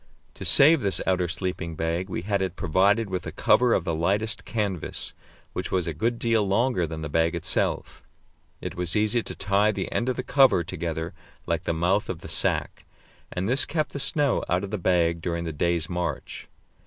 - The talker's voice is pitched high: No, very low, 95 Hz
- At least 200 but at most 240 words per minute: Yes, fast, 205 wpm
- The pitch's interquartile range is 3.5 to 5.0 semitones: Yes, average, 4.2 semitones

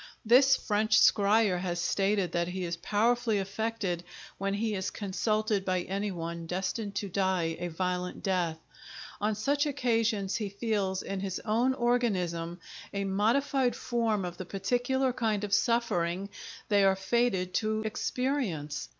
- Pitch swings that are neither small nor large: Yes, average, 3.7 semitones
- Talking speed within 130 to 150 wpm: Yes, average, 145 wpm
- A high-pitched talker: Yes, high, 200 Hz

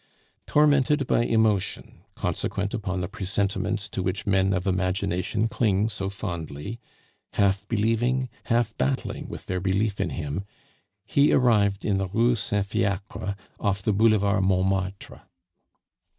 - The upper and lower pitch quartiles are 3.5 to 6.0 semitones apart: No, average, 2.8 semitones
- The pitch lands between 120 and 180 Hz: No, low, 100 Hz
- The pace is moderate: No, slow, 130 wpm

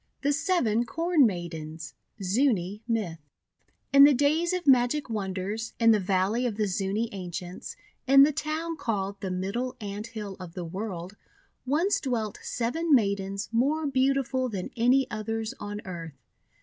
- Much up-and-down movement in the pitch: Yes, wide, 5.9 semitones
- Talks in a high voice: Yes, high, 225 Hz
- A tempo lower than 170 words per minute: Yes, average, 150 wpm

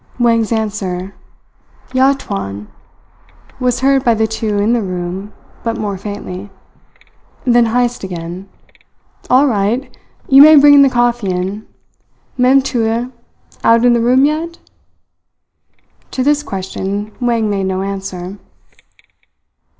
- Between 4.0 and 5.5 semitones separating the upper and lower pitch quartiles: Yes, average, 4.3 semitones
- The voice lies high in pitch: Yes, high, 225 Hz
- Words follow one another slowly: Yes, slow, 120 wpm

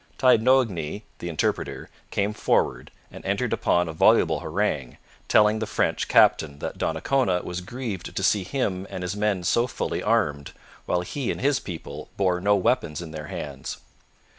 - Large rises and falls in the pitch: No, average, 4.3 semitones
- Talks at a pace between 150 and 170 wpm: Yes, average, 165 wpm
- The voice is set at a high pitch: No, very low, 95 Hz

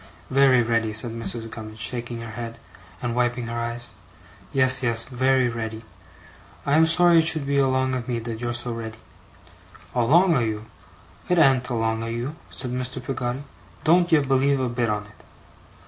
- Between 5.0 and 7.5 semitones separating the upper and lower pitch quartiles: No, narrow, 2.4 semitones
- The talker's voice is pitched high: No, low, 120 Hz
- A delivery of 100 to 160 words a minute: No, average, 180 wpm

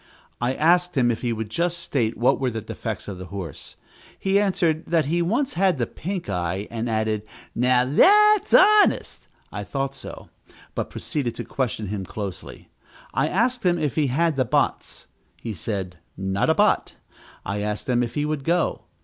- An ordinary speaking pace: Yes, average, 185 wpm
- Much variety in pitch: Yes, wide, 8.0 semitones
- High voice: No, low, 130 Hz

